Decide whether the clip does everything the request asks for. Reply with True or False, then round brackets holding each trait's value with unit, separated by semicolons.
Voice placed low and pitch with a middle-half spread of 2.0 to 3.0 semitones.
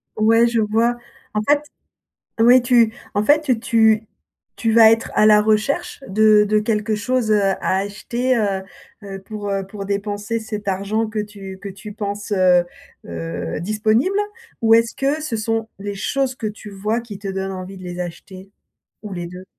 False (215 Hz; 2.6 semitones)